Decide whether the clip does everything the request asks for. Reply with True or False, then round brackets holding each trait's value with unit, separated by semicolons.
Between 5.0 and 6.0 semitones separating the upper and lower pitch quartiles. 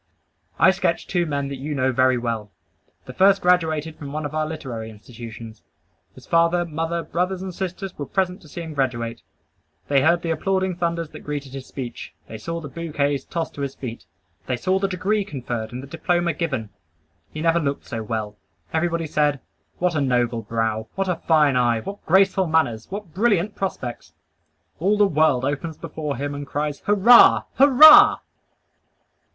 True (5.3 semitones)